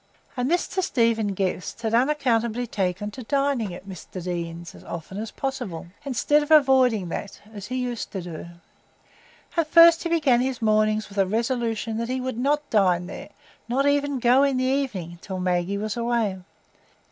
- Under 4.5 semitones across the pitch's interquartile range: No, average, 5.2 semitones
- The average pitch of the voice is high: Yes, high, 230 Hz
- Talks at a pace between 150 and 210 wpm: Yes, average, 175 wpm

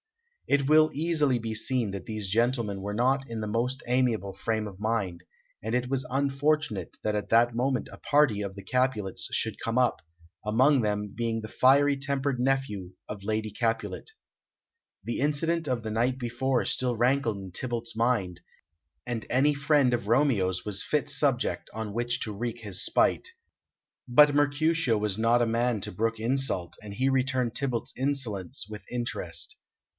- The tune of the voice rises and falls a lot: No, average, 3.9 semitones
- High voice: No, low, 120 Hz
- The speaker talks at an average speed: Yes, average, 170 wpm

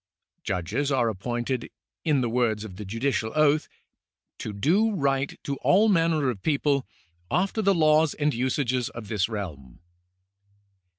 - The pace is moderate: Yes, average, 150 wpm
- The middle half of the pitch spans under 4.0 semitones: No, wide, 5.6 semitones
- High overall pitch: No, low, 130 Hz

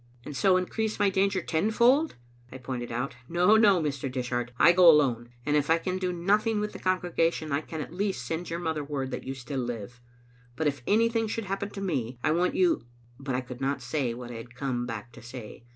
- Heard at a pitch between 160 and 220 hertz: No, medium, 150 Hz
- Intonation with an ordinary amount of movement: No, wide, 6.9 semitones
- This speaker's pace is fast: Yes, fast, 235 wpm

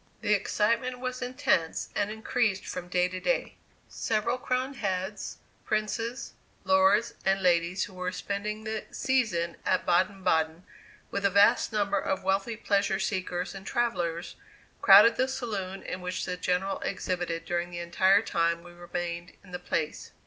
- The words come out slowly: No, average, 155 wpm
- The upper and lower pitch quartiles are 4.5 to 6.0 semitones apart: No, average, 3.5 semitones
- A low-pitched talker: No, high, 195 Hz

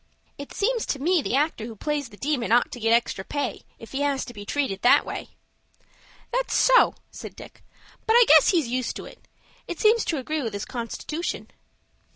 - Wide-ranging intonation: Yes, wide, 5.8 semitones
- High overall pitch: Yes, very high, 280 Hz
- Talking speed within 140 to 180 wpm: No, average, 200 wpm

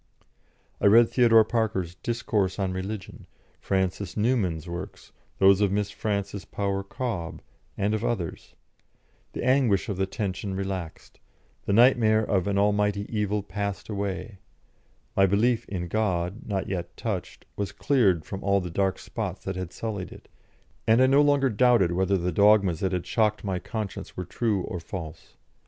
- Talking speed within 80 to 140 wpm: No, average, 160 wpm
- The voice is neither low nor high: No, low, 100 Hz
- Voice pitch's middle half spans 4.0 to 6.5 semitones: No, average, 2.7 semitones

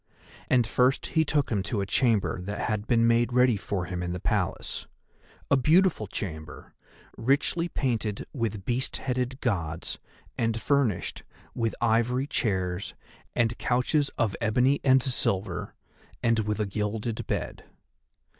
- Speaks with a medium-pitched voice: No, low, 115 Hz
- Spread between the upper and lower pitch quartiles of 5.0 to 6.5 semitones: No, average, 3.8 semitones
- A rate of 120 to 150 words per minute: Yes, average, 140 wpm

